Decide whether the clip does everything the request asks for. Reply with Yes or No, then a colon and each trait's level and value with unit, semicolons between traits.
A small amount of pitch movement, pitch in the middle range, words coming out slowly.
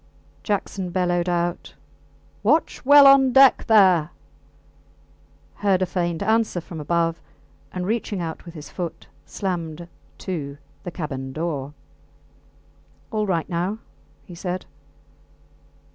No: average, 3.3 semitones; medium, 175 Hz; slow, 115 wpm